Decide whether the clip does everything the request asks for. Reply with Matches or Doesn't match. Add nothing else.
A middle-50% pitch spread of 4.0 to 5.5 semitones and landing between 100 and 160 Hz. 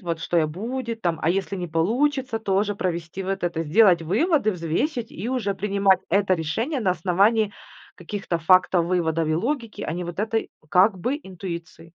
Doesn't match